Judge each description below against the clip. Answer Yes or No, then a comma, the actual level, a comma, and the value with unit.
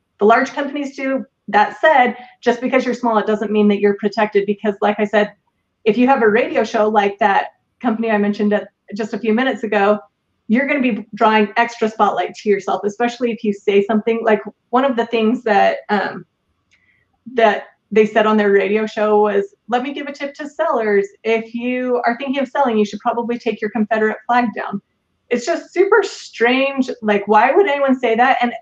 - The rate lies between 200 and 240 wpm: Yes, fast, 205 wpm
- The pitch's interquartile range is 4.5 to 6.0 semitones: No, average, 2.9 semitones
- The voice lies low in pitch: No, high, 225 Hz